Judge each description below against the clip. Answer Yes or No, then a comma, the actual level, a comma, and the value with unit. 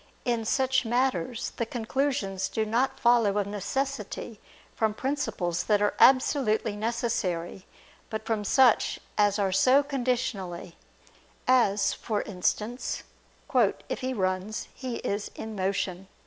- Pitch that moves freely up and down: No, average, 4.2 semitones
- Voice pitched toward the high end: Yes, high, 220 Hz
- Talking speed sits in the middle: No, slow, 120 wpm